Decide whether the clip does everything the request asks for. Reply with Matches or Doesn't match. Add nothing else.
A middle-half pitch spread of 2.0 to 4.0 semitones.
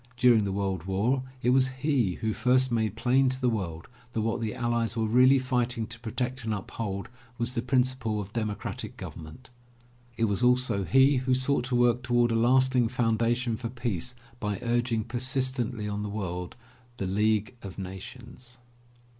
Matches